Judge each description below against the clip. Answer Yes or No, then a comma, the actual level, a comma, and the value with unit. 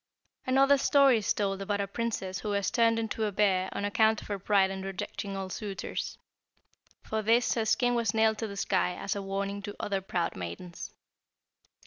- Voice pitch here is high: Yes, high, 205 Hz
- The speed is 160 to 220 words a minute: Yes, average, 190 wpm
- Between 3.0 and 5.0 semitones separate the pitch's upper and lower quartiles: No, narrow, 2.4 semitones